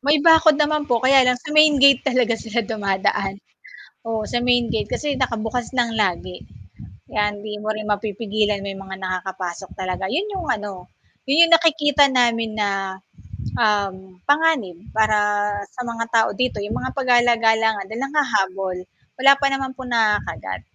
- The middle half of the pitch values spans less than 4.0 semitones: No, average, 4.4 semitones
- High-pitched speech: Yes, high, 225 Hz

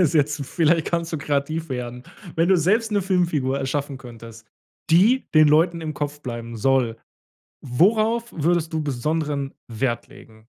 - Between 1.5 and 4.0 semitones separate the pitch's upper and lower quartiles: No, average, 4.4 semitones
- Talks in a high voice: No, medium, 150 Hz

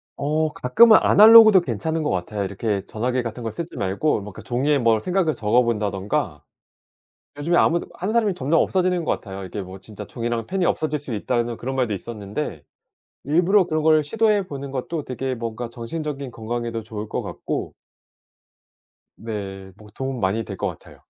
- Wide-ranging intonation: Yes, wide, 6.7 semitones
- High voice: No, low, 125 Hz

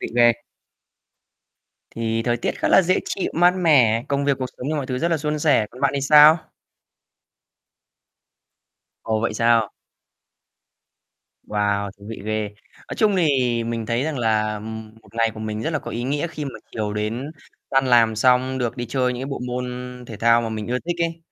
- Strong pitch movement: No, average, 4.3 semitones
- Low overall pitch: Yes, low, 125 Hz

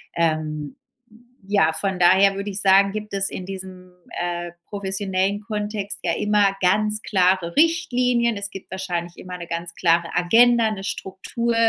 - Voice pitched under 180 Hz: No, high, 195 Hz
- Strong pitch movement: No, average, 2.8 semitones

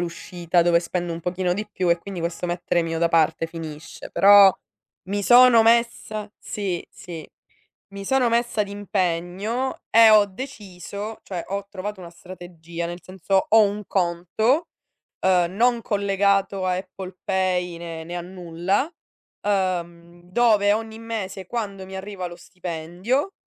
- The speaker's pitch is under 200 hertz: Yes, high, 190 Hz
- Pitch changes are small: No, average, 3.2 semitones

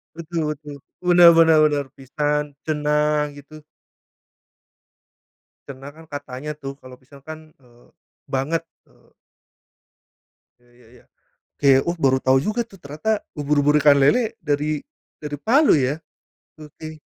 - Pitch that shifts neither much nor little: No, narrow, 2.2 semitones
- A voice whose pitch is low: No, medium, 150 Hz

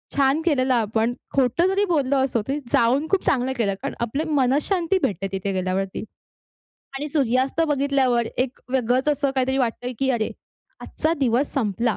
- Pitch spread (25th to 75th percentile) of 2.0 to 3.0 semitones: No, average, 3.4 semitones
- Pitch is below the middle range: No, very high, 260 Hz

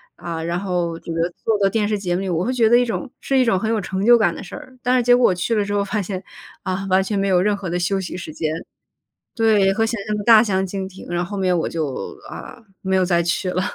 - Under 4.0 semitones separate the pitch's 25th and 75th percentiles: Yes, average, 3.4 semitones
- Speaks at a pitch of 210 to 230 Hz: No, high, 195 Hz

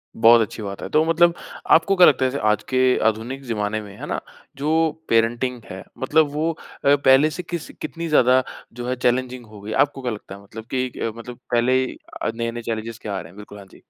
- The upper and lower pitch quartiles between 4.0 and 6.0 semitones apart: Yes, average, 4.3 semitones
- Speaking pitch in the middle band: No, low, 125 Hz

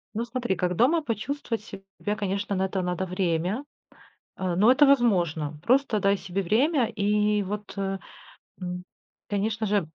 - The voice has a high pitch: Yes, high, 200 Hz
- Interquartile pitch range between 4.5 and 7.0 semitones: No, average, 3.6 semitones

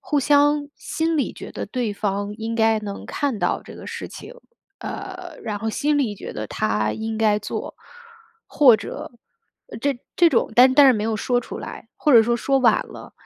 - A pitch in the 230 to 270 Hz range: Yes, high, 235 Hz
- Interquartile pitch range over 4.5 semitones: Yes, average, 5.0 semitones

